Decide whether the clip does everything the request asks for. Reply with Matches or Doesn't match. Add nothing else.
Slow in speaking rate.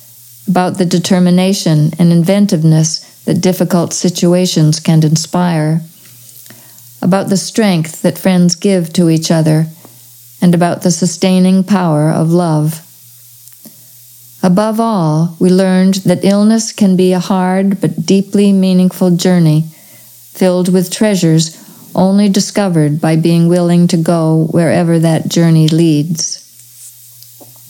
Matches